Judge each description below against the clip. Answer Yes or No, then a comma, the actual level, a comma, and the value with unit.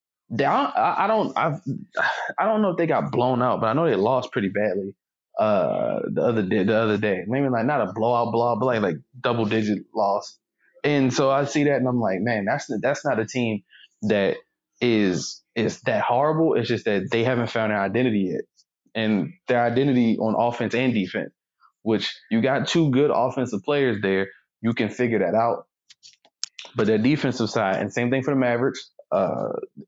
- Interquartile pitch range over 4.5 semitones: No, average, 3.6 semitones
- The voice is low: Yes, low, 120 Hz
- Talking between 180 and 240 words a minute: Yes, average, 200 wpm